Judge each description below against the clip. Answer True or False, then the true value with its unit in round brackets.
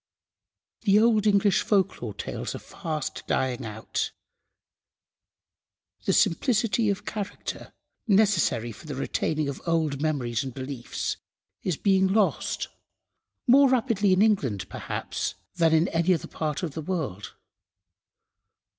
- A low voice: False (170 Hz)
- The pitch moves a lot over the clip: True (6.8 semitones)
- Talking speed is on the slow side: True (120 wpm)